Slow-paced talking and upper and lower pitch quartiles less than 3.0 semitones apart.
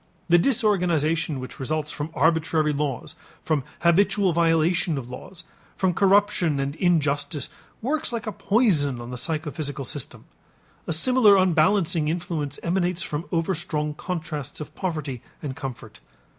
No: slow, 130 wpm; average, 3.7 semitones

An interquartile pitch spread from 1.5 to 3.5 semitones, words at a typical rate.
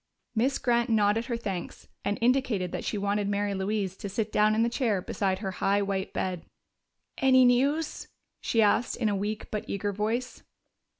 Yes: average, 3.0 semitones; average, 180 wpm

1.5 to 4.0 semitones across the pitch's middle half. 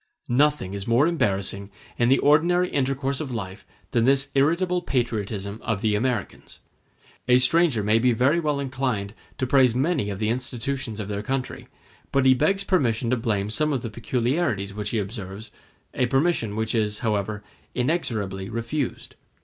No: average, 4.6 semitones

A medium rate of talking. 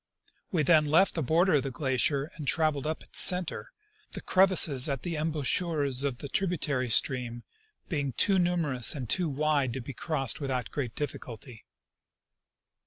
Yes: average, 160 wpm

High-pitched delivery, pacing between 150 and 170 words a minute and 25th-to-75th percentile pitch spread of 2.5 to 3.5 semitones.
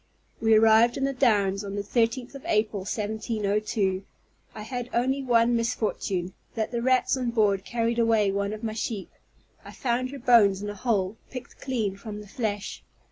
No: high, 220 Hz; average, 180 wpm; average, 2.8 semitones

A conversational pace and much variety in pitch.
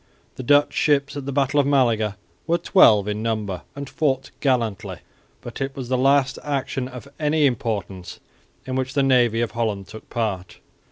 No: average, 175 wpm; average, 4.2 semitones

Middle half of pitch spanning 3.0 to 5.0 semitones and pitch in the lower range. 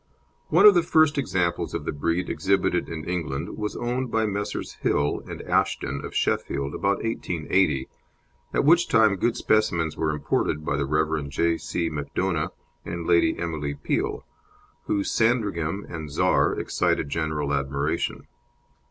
No: wide, 5.4 semitones; very low, 85 Hz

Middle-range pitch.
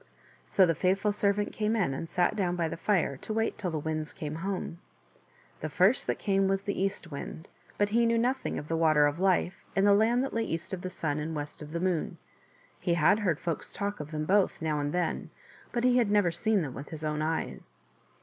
Yes: medium, 180 Hz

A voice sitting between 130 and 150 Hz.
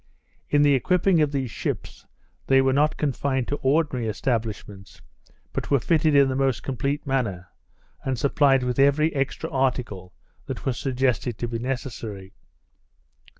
Yes: low, 135 Hz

